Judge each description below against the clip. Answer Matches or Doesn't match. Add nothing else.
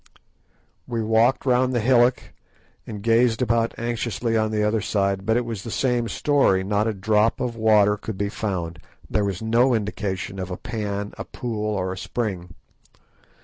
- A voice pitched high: Doesn't match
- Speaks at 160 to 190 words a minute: Matches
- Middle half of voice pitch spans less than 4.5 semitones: Matches